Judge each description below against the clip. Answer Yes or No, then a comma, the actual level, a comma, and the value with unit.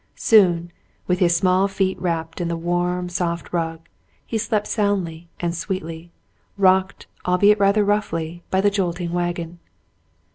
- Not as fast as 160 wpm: Yes, average, 140 wpm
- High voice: No, medium, 175 Hz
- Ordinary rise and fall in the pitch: No, narrow, 2.3 semitones